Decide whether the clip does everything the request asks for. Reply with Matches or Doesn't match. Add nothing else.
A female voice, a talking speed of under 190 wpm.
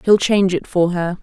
Doesn't match